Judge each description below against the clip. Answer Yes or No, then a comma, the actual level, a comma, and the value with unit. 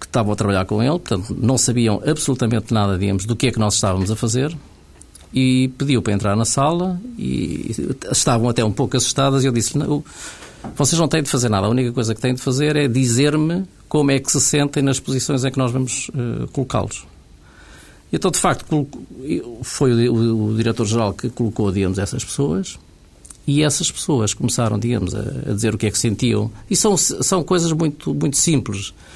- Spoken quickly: Yes, fast, 200 wpm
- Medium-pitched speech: No, low, 125 Hz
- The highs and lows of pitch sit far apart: No, average, 4.9 semitones